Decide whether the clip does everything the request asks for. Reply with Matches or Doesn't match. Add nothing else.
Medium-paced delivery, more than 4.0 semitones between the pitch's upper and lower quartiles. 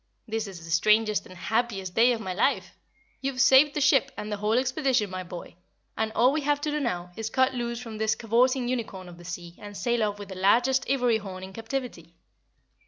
Doesn't match